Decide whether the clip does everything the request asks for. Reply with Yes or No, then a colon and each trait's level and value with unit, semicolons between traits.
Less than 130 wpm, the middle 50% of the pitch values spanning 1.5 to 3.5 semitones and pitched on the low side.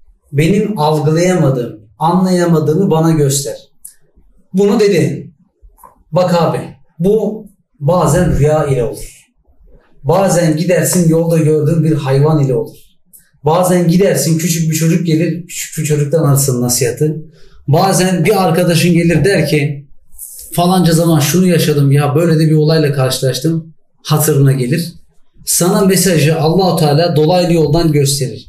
No: average, 120 wpm; average, 2.8 semitones; medium, 160 Hz